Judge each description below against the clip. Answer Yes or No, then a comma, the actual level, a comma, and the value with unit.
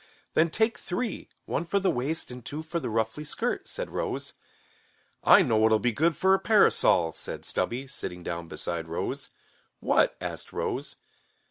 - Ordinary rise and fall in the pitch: No, wide, 8.9 semitones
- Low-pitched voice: No, medium, 145 Hz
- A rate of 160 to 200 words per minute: Yes, average, 165 wpm